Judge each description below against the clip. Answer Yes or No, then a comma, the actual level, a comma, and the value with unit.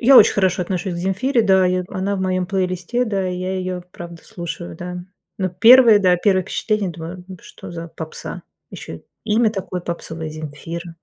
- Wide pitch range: No, narrow, 2.4 semitones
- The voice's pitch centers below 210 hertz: Yes, medium, 185 Hz